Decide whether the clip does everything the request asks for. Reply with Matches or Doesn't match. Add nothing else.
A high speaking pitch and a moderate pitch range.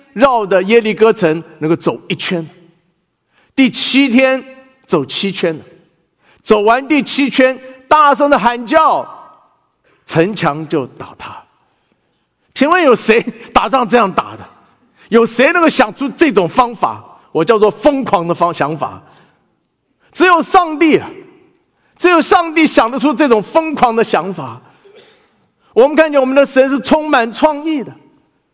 Doesn't match